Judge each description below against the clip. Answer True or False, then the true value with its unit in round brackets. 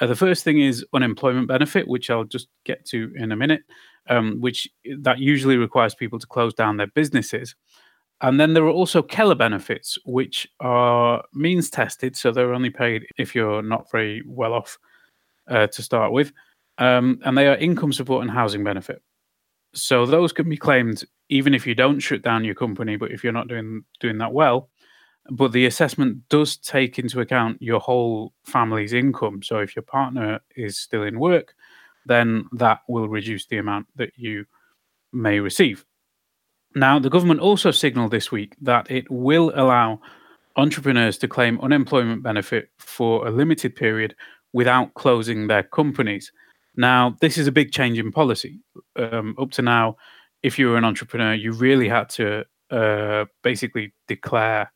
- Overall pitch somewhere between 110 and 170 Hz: True (125 Hz)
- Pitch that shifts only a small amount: False (3.3 semitones)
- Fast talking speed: True (175 wpm)